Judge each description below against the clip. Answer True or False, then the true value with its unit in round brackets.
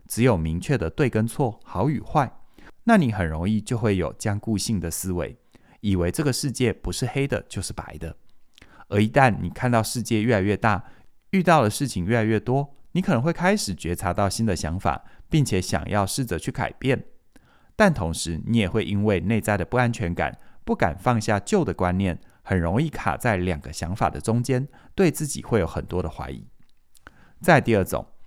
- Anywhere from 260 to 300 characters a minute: True (280 characters per minute)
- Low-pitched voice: True (105 Hz)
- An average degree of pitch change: False (5.7 semitones)